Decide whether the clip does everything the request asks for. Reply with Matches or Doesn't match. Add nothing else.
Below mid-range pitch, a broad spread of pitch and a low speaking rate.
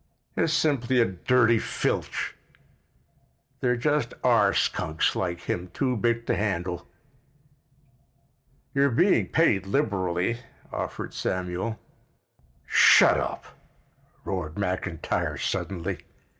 Matches